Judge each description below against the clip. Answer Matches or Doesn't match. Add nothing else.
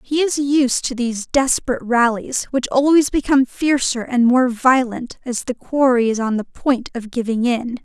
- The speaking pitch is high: Matches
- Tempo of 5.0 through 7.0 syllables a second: Doesn't match